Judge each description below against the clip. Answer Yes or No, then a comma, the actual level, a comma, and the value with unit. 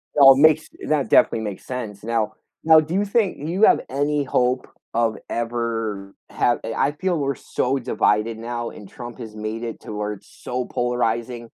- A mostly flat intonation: No, average, 4.1 semitones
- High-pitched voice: No, low, 120 Hz